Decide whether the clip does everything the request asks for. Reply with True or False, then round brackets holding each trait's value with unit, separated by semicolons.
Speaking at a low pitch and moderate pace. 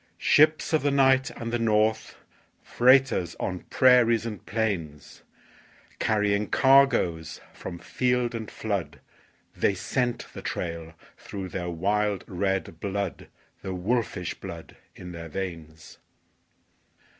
False (100 Hz; 115 wpm)